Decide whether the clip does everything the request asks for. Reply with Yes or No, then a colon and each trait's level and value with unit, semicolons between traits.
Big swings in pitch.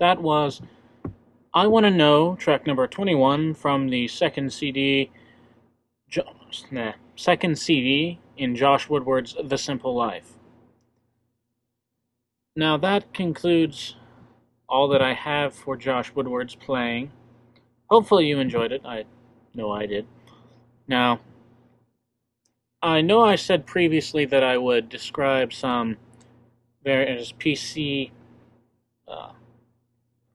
No: average, 3.6 semitones